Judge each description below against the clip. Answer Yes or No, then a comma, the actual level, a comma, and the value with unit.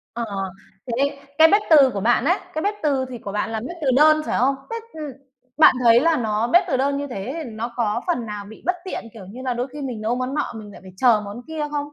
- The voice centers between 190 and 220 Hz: No, very high, 255 Hz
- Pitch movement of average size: Yes, average, 5.0 semitones